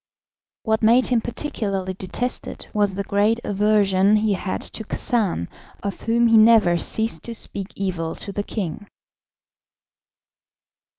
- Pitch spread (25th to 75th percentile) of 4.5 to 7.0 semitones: No, average, 2.7 semitones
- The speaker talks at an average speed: No, slow, 130 wpm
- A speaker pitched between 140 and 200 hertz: No, high, 210 Hz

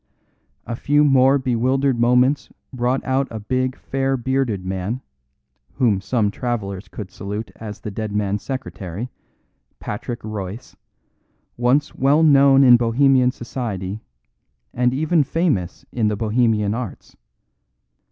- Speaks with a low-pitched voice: Yes, low, 120 Hz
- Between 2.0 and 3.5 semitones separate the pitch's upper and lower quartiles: No, average, 4.1 semitones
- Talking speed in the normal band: No, slow, 125 wpm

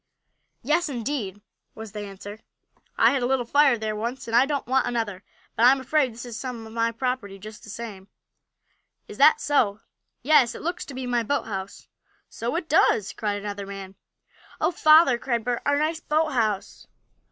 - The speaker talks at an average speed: Yes, average, 180 wpm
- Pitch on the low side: No, high, 235 Hz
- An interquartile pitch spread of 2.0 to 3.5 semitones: No, average, 4.4 semitones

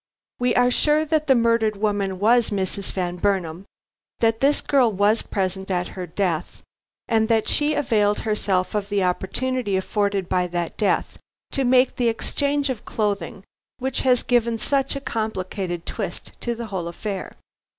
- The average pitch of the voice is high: Yes, high, 210 Hz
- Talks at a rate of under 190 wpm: Yes, average, 160 wpm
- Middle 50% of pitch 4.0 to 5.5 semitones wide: Yes, average, 4.4 semitones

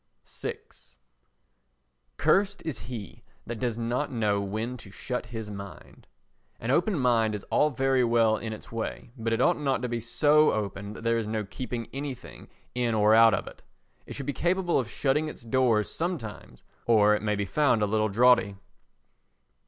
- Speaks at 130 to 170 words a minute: No, average, 180 wpm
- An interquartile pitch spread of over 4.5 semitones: No, average, 3.5 semitones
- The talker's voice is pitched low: Yes, low, 115 Hz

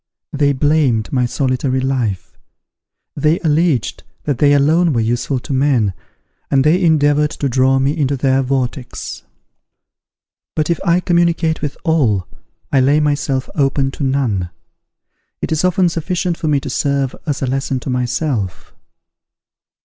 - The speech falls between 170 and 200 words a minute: No, average, 145 wpm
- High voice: No, medium, 140 Hz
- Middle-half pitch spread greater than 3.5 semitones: No, average, 2.9 semitones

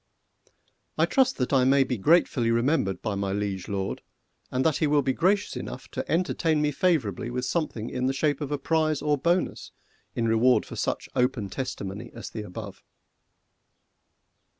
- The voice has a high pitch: No, low, 130 Hz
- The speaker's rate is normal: Yes, average, 170 wpm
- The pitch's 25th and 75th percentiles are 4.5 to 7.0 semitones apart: Yes, average, 5.3 semitones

